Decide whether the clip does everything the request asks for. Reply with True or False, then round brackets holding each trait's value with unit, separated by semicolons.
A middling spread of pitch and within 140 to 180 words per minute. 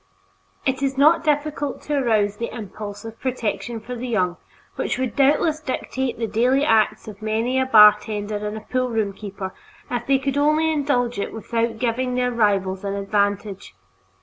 True (4.0 semitones; 165 wpm)